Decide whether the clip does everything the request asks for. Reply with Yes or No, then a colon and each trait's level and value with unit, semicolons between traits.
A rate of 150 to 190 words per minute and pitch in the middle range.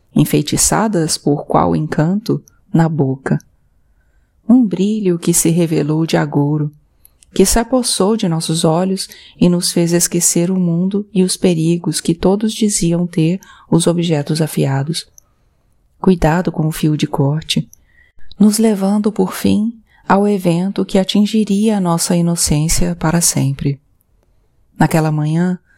No: average, 130 wpm; medium, 170 Hz